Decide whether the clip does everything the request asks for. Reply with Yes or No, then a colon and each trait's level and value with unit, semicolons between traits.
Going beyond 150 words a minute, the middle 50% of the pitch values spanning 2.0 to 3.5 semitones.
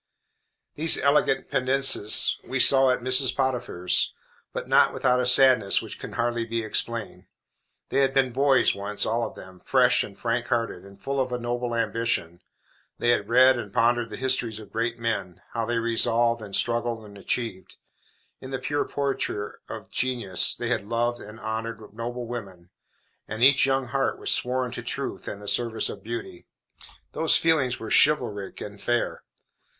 Yes: average, 170 wpm; average, 2.8 semitones